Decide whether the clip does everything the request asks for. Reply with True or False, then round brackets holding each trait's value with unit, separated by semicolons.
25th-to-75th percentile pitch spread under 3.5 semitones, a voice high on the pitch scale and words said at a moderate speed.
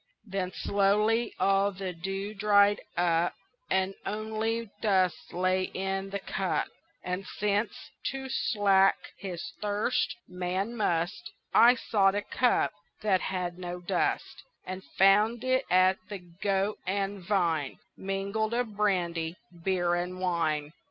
False (2.4 semitones; 195 Hz; 125 wpm)